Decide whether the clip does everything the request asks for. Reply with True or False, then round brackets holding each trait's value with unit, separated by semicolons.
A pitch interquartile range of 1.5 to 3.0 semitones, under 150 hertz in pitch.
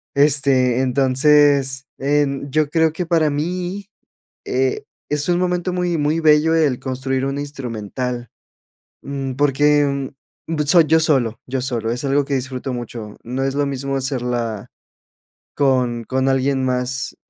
True (2.5 semitones; 135 Hz)